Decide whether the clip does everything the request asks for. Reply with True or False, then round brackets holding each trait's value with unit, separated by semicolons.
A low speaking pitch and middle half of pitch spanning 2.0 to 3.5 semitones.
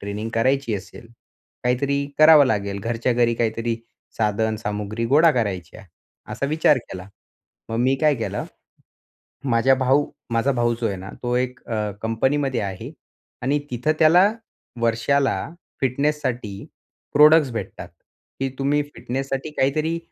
False (125 Hz; 4.0 semitones)